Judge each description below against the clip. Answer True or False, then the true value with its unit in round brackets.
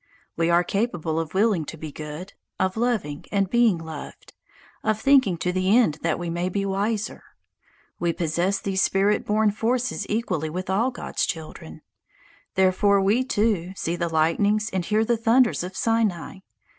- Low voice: False (195 Hz)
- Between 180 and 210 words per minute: False (165 wpm)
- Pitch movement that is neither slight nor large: True (4.1 semitones)